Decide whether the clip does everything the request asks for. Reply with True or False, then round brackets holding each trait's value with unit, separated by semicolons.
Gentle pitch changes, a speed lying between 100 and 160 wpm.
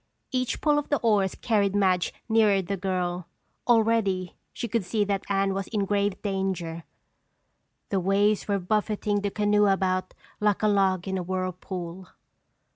True (2.0 semitones; 155 wpm)